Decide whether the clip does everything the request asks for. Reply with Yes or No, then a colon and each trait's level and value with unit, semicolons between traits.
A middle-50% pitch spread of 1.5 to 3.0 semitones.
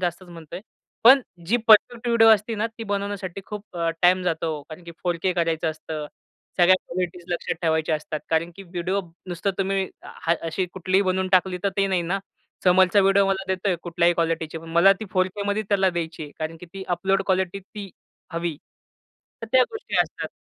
Yes: average, 2.7 semitones